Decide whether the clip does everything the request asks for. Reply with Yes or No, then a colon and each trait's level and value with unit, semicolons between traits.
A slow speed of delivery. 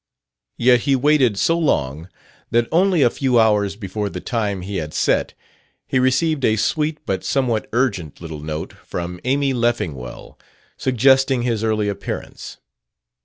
No: average, 145 wpm